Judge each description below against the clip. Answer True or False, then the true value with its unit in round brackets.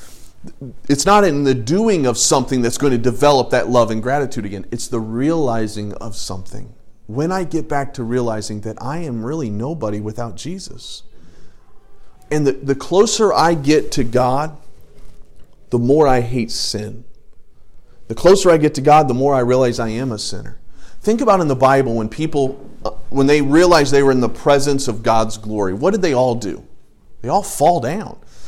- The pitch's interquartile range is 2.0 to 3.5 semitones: False (4.3 semitones)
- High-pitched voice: False (130 Hz)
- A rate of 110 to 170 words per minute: False (185 wpm)